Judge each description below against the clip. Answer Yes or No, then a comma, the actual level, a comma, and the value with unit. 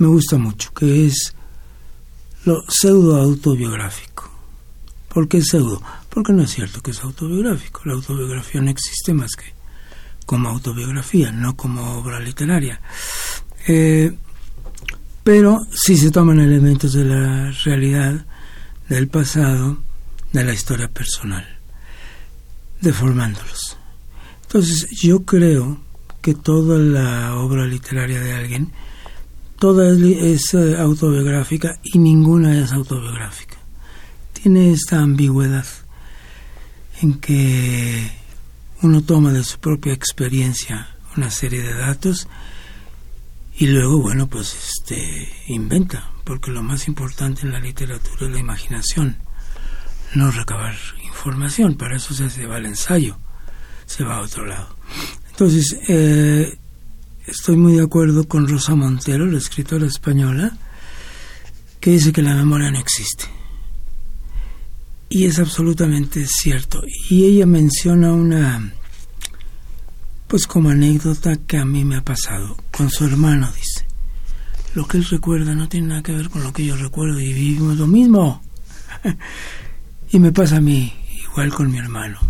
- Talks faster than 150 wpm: No, average, 130 wpm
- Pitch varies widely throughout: Yes, wide, 6.8 semitones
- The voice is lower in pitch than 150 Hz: Yes, low, 135 Hz